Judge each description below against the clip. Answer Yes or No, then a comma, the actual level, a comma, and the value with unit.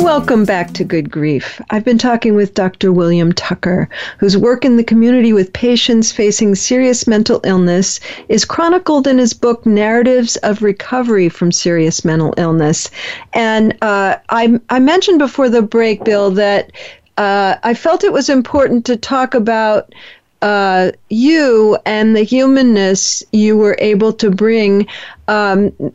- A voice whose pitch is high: Yes, high, 220 Hz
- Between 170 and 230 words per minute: No, average, 150 wpm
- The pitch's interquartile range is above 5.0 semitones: No, average, 3.9 semitones